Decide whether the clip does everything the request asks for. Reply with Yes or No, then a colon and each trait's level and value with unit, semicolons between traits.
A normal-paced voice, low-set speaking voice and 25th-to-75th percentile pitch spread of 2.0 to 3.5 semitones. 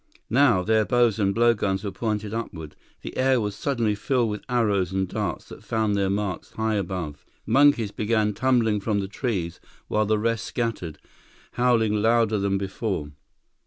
Yes: average, 160 wpm; low, 105 Hz; average, 2.9 semitones